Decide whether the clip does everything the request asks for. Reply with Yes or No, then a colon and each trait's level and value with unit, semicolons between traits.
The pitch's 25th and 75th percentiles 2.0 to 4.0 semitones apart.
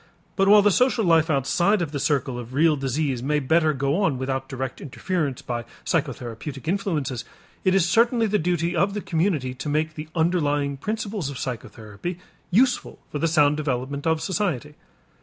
No: average, 5.0 semitones